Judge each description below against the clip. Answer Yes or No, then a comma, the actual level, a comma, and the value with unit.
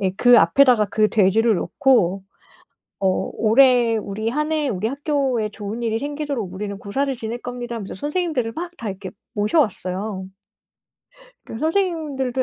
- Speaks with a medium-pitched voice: No, high, 235 Hz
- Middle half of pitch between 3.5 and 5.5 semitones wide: Yes, average, 5.1 semitones